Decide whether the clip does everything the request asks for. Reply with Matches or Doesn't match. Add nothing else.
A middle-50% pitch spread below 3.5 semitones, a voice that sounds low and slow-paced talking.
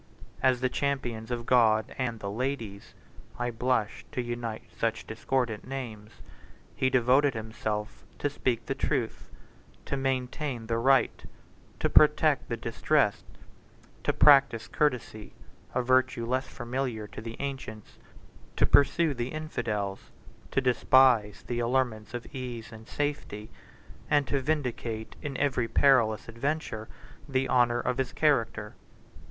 Matches